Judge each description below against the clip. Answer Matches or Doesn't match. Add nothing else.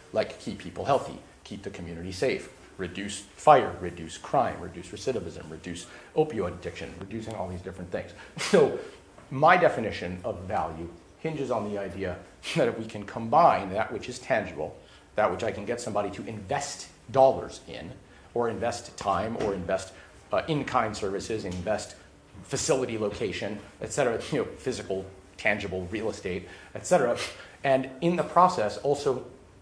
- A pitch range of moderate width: Matches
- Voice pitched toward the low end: Matches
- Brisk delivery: Doesn't match